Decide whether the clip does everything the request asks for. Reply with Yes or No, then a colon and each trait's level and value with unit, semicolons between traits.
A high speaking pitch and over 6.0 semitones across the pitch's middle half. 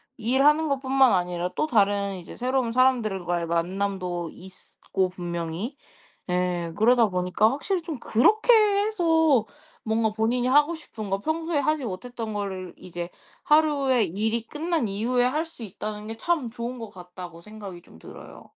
Yes: high, 225 Hz; wide, 6.8 semitones